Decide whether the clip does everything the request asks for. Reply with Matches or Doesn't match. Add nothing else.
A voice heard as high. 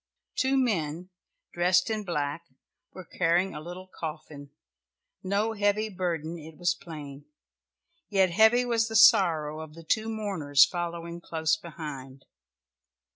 Doesn't match